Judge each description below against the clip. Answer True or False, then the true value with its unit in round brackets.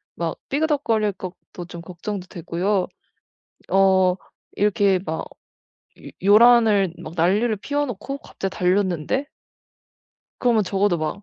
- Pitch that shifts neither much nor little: True (3.5 semitones)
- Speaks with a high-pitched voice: True (195 Hz)